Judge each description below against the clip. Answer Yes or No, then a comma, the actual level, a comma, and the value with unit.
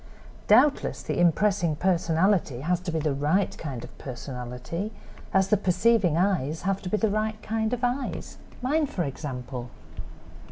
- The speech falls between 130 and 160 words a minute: Yes, average, 150 wpm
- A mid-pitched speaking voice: Yes, medium, 180 Hz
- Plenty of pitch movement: Yes, wide, 6.3 semitones